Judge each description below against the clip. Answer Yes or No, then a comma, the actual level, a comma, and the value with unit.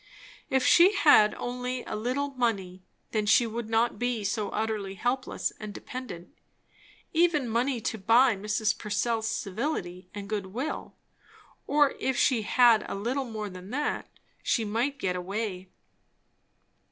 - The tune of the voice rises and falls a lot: No, average, 3.7 semitones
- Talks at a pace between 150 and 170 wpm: No, average, 140 wpm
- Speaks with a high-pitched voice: Yes, high, 225 Hz